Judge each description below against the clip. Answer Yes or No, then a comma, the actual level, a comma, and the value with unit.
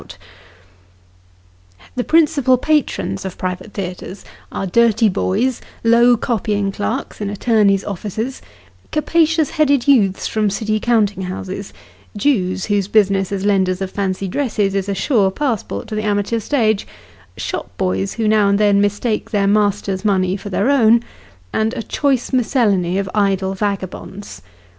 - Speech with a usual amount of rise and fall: Yes, average, 3.3 semitones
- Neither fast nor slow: Yes, average, 150 wpm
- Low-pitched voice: No, high, 205 Hz